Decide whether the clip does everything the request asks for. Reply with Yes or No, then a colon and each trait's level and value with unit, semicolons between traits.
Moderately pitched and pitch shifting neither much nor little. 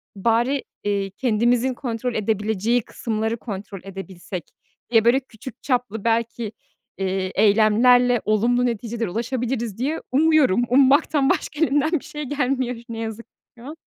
No: high, 235 Hz; average, 3.2 semitones